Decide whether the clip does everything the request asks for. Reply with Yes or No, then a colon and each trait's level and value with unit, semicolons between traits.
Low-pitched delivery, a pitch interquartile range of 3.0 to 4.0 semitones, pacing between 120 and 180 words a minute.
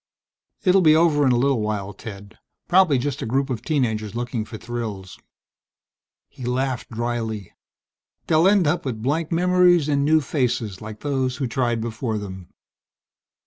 No: low, 125 Hz; average, 5.1 semitones; average, 165 wpm